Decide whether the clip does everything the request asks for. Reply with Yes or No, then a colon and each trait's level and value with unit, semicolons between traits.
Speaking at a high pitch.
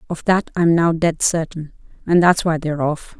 No: medium, 165 Hz